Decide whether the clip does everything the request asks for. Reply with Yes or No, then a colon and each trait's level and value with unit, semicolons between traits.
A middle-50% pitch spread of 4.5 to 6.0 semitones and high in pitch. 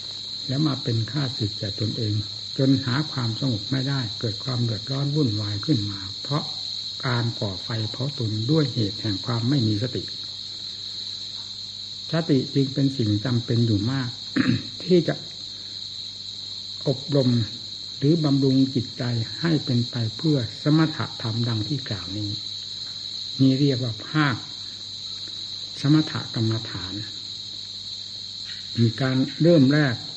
No: average, 4.8 semitones; low, 115 Hz